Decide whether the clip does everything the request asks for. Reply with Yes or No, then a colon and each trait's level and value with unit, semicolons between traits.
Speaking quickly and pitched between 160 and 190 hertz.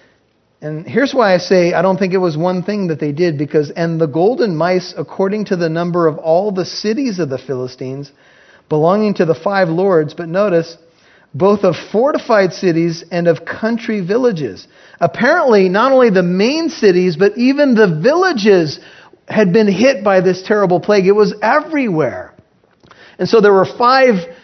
No: average, 175 wpm; medium, 185 Hz